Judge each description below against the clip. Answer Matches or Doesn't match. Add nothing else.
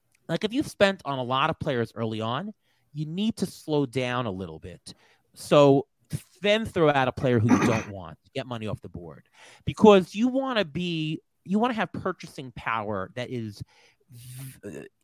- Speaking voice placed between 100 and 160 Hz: Matches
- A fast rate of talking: Doesn't match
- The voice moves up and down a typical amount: Doesn't match